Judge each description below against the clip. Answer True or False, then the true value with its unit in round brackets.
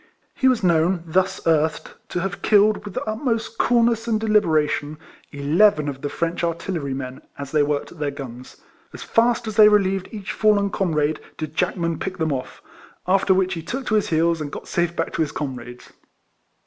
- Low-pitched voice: False (175 Hz)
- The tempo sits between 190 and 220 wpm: True (195 wpm)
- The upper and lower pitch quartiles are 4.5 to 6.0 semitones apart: True (5.6 semitones)